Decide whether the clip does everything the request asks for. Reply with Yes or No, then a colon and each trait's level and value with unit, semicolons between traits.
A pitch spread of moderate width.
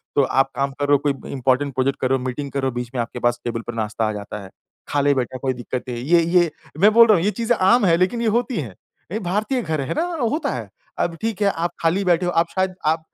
No: wide, 6.5 semitones